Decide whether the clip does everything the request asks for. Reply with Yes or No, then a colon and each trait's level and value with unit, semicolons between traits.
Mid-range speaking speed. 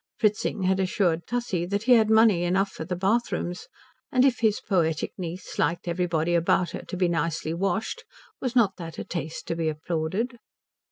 Yes: average, 180 wpm